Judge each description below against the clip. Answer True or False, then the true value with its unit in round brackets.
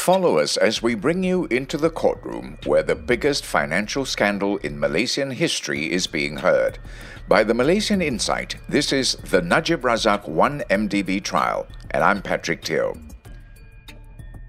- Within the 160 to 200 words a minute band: False (145 wpm)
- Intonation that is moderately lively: False (7.5 semitones)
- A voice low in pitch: True (120 Hz)